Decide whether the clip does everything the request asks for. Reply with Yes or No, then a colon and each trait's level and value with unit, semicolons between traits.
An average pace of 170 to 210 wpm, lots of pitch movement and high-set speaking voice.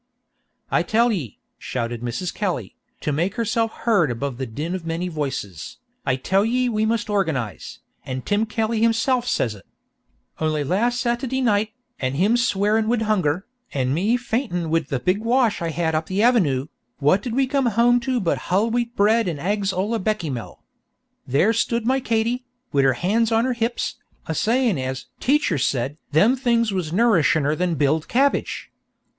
Yes: average, 175 wpm; wide, 7.2 semitones; high, 200 Hz